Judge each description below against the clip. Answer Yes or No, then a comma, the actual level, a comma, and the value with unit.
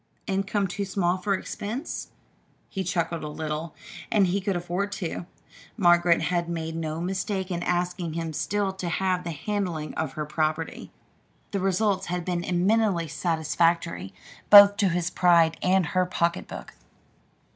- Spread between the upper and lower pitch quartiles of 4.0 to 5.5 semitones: No, narrow, 2.6 semitones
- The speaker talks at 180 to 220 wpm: No, average, 145 wpm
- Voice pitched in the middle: Yes, medium, 175 Hz